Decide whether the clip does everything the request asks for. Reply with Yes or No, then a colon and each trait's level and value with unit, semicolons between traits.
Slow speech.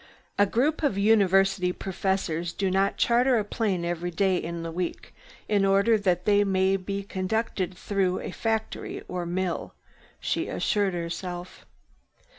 No: average, 145 wpm